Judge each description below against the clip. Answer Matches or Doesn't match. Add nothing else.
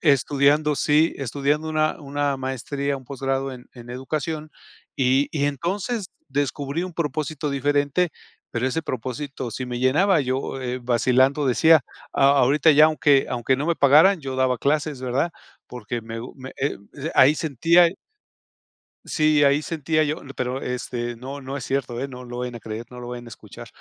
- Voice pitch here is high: Doesn't match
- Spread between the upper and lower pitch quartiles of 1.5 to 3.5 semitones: Matches